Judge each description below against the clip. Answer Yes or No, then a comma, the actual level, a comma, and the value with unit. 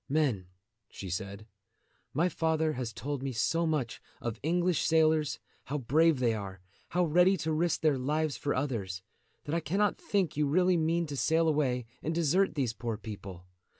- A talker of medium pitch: Yes, medium, 150 Hz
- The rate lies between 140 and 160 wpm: No, average, 175 wpm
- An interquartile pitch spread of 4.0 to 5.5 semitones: Yes, average, 5.1 semitones